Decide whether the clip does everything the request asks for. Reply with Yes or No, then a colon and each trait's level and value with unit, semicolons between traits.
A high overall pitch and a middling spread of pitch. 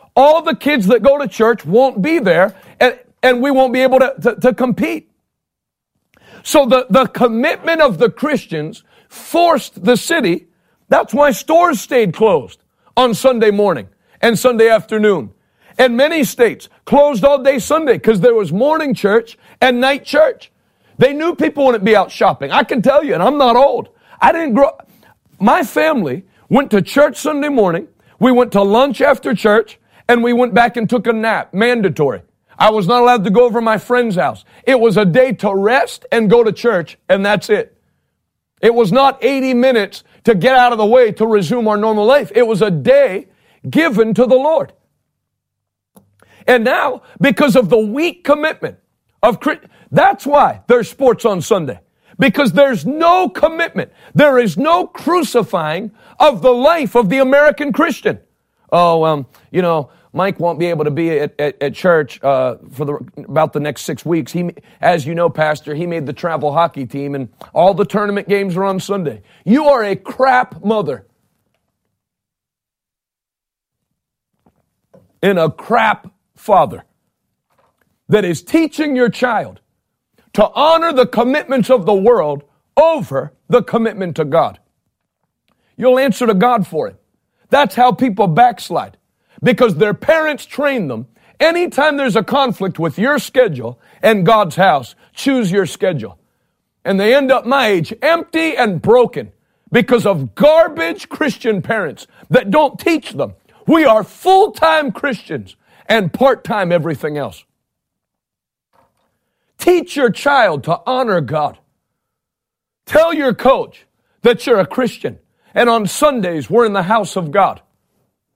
No: high, 240 Hz; wide, 5.9 semitones